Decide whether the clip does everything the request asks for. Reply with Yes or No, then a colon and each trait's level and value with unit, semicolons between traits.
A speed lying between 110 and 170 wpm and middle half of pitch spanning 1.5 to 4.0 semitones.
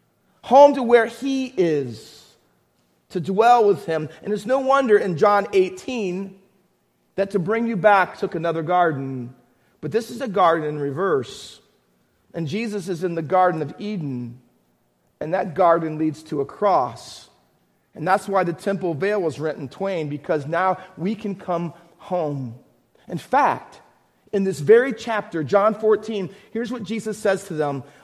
No: average, 165 wpm; average, 5.2 semitones